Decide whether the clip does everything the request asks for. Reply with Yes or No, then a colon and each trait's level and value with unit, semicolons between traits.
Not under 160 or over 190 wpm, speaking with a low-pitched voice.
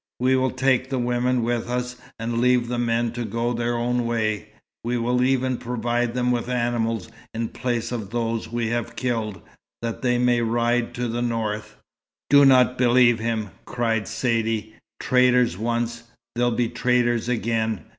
Yes: average, 165 wpm; low, 120 Hz